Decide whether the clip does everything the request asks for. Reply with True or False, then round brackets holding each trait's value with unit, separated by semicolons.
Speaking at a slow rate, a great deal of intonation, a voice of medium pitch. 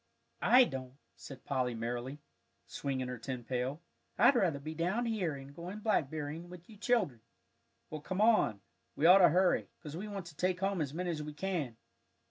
False (185 wpm; 5.8 semitones; 160 Hz)